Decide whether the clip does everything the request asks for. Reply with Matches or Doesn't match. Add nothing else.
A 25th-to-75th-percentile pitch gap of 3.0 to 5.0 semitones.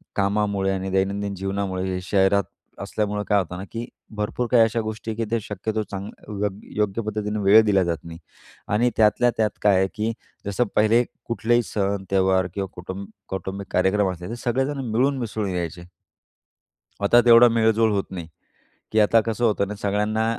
Doesn't match